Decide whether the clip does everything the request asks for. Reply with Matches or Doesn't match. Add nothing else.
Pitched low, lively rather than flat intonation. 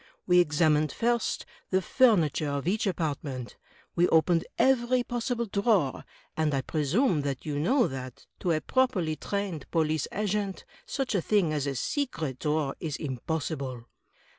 Doesn't match